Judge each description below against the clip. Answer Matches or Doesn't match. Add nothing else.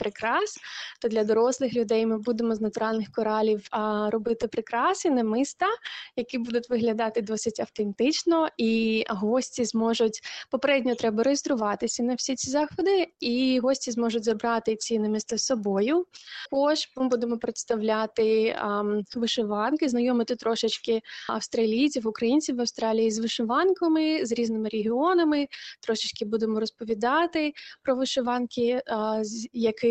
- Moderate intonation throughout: Matches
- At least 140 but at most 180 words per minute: Doesn't match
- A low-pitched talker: Doesn't match